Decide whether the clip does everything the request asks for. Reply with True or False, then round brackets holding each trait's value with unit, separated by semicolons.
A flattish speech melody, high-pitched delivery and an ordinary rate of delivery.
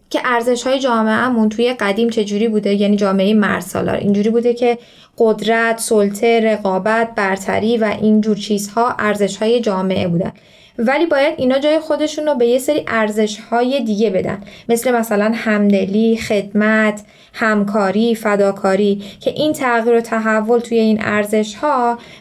True (2.3 semitones; 220 Hz; 145 wpm)